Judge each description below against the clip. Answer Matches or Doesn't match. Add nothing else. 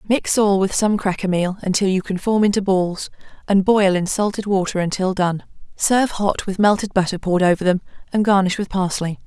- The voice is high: Matches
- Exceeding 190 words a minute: Matches